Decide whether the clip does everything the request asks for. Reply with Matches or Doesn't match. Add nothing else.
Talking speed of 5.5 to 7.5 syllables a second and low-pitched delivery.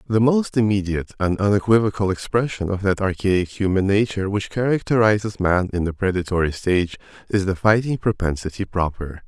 Matches